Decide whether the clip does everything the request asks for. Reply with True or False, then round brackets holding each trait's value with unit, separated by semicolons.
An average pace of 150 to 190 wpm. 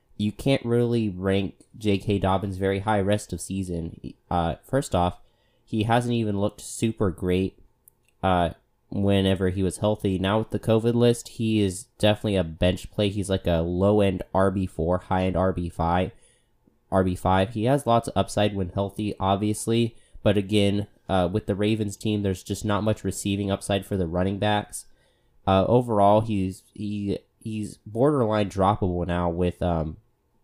True (165 wpm)